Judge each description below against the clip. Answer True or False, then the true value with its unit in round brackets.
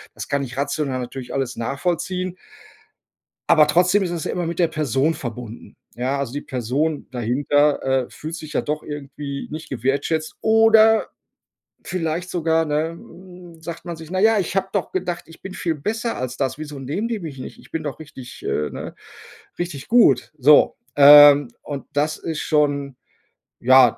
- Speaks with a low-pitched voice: False (150 Hz)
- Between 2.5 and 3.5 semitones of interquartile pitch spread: False (4.0 semitones)